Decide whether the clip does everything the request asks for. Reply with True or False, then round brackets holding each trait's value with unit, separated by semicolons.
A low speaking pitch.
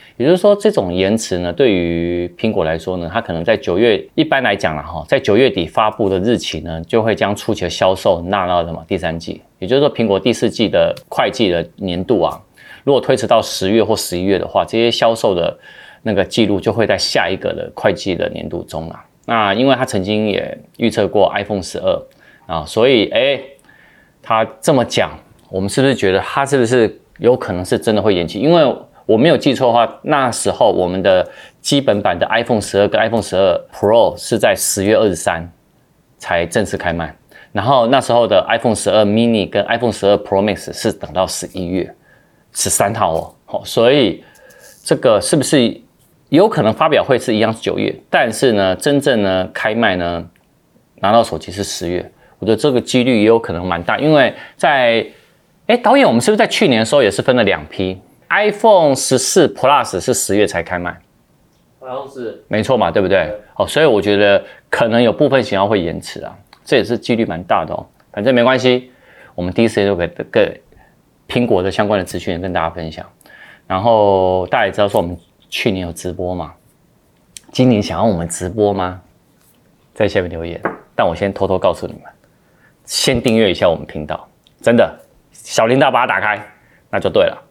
True (100 Hz)